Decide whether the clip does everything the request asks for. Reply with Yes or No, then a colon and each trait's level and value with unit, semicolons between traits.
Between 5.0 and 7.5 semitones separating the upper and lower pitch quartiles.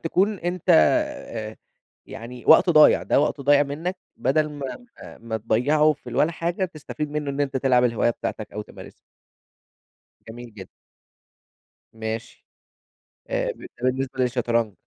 Yes: wide, 5.4 semitones